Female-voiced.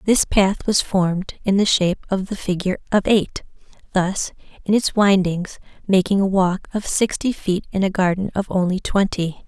Yes: female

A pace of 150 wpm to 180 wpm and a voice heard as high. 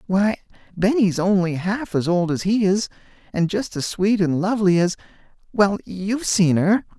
Yes: average, 165 wpm; high, 195 Hz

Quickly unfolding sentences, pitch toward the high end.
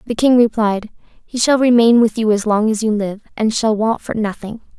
Yes: fast, 225 wpm; high, 220 Hz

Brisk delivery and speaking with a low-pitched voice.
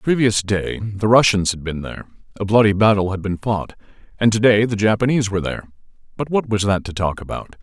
Yes: fast, 210 wpm; low, 105 Hz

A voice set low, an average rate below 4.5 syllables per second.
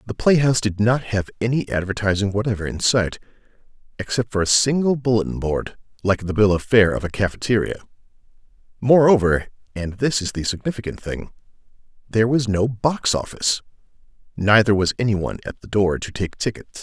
No: low, 105 Hz; 5.8 syllables/s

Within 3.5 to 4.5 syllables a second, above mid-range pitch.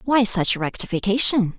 No: 4.7 syllables/s; high, 210 Hz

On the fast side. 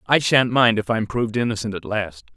Yes: fast, 230 wpm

